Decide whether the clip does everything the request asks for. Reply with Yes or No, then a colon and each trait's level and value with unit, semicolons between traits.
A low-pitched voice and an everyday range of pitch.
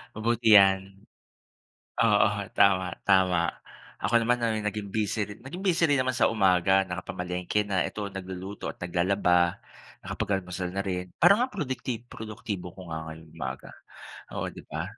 Yes: very low, 95 Hz; average, 3.7 semitones